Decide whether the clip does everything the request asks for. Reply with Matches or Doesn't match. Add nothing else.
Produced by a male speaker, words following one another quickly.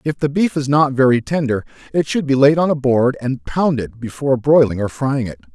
Matches